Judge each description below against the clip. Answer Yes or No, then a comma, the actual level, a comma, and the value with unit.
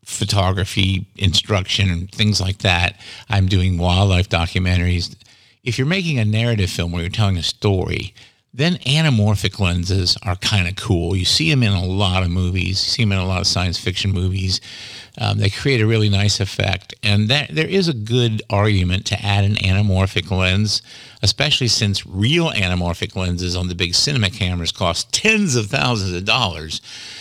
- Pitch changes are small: No, average, 3.3 semitones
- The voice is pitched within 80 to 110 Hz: Yes, low, 100 Hz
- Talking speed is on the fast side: No, average, 180 wpm